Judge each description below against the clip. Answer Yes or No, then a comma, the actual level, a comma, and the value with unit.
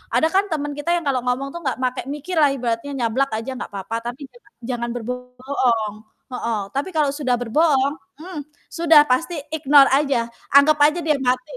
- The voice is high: Yes, very high, 275 Hz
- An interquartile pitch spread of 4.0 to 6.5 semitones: No, average, 3.6 semitones